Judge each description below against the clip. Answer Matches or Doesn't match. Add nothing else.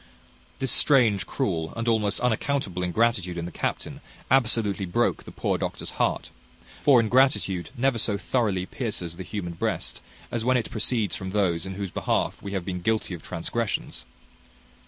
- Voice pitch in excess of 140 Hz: Doesn't match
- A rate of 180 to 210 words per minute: Doesn't match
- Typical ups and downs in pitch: Matches